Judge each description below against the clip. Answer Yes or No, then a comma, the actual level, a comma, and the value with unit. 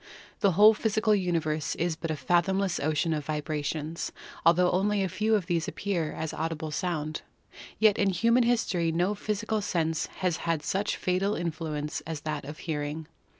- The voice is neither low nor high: Yes, medium, 170 Hz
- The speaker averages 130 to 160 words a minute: No, average, 170 wpm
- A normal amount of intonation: Yes, average, 4.2 semitones